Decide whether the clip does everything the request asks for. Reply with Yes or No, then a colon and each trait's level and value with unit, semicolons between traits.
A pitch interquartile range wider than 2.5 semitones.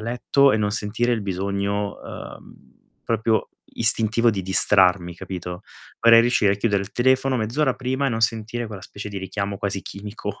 Yes: average, 2.9 semitones